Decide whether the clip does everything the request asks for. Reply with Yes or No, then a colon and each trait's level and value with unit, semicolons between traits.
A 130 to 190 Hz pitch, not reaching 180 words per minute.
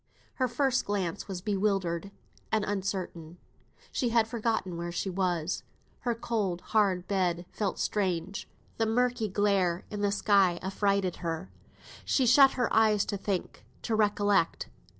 No: high, 200 Hz; average, 140 wpm